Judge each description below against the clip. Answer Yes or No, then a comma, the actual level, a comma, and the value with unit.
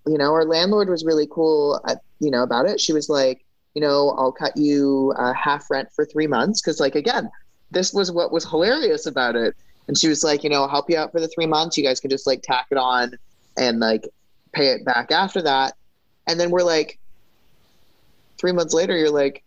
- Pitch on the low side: No, medium, 150 Hz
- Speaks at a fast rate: Yes, fast, 230 wpm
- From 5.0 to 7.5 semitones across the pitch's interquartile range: No, average, 3.7 semitones